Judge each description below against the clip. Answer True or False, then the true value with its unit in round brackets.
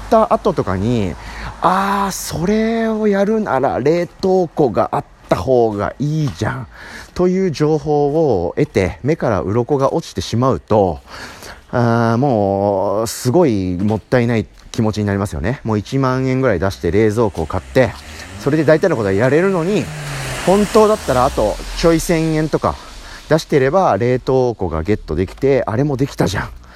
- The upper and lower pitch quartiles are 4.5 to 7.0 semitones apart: False (7.8 semitones)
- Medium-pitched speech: False (130 Hz)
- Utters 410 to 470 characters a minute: False (310 characters per minute)